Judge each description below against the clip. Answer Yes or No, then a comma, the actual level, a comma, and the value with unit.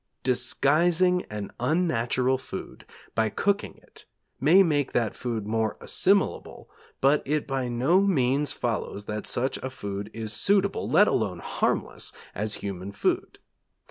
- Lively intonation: Yes, wide, 6.6 semitones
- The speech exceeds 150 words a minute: No, slow, 135 wpm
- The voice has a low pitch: Yes, low, 130 Hz